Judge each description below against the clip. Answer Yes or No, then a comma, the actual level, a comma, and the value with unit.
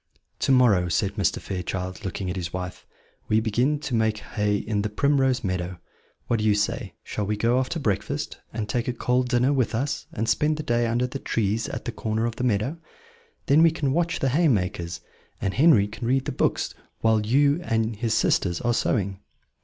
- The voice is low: Yes, low, 115 Hz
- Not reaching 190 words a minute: No, average, 200 wpm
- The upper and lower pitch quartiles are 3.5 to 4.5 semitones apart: Yes, average, 4.1 semitones